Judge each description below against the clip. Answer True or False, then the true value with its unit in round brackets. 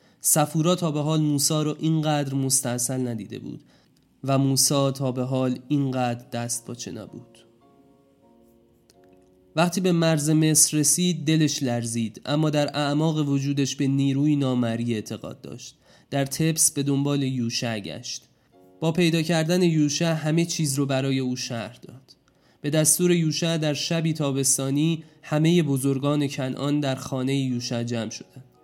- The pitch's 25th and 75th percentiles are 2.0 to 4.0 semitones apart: True (3.6 semitones)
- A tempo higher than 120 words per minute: True (140 wpm)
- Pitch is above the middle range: False (140 Hz)